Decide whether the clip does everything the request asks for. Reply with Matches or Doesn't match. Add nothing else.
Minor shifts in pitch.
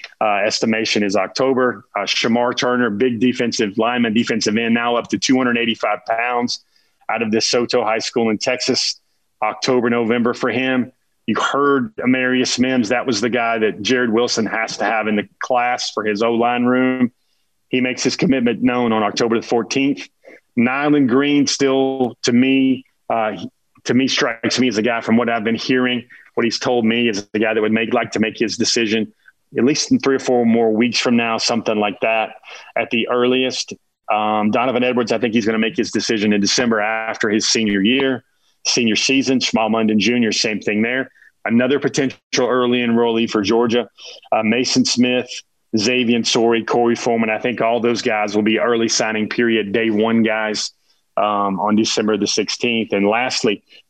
Matches